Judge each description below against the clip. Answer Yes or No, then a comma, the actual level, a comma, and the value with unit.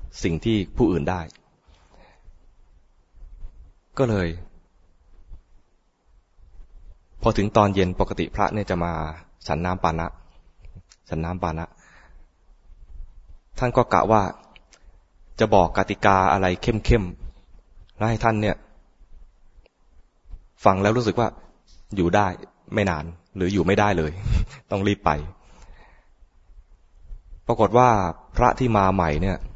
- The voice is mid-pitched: No, very low, 90 Hz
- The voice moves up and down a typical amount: Yes, average, 4.1 semitones